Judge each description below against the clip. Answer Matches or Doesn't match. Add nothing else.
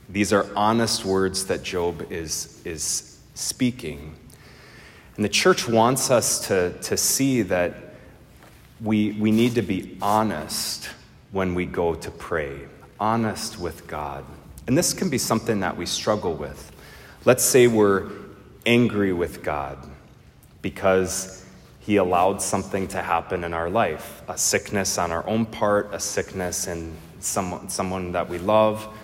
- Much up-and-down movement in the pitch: Doesn't match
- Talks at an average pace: Matches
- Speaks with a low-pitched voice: Matches